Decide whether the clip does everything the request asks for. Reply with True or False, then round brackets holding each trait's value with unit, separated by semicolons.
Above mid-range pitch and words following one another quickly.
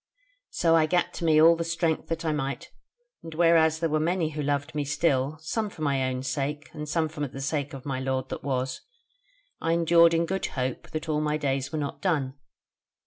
False (155 Hz; 215 wpm)